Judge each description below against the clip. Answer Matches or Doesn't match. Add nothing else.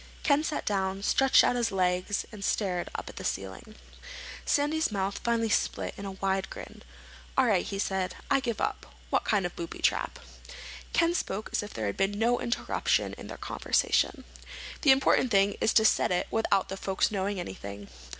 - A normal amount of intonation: Matches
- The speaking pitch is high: Matches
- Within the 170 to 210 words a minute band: Matches